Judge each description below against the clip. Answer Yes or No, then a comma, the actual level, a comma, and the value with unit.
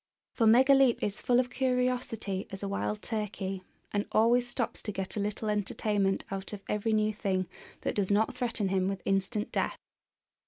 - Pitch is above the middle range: Yes, high, 210 Hz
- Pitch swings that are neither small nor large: Yes, average, 3.1 semitones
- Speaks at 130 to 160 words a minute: No, average, 175 wpm